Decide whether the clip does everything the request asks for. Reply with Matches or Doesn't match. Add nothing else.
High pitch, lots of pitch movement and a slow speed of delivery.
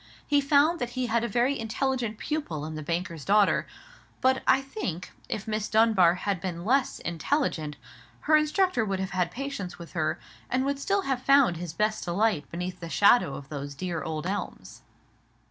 Doesn't match